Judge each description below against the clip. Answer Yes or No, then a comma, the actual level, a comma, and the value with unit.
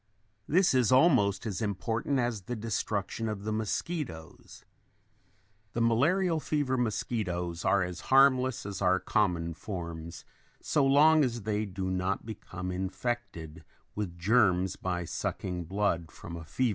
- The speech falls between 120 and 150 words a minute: Yes, average, 140 wpm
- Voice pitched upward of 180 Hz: No, low, 105 Hz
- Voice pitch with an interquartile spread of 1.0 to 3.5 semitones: No, wide, 5.4 semitones